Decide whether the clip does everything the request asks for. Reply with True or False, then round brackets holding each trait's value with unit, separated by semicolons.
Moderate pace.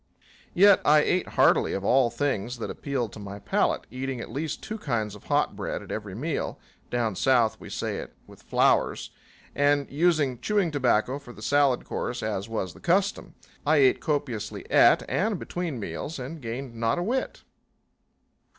True (175 wpm)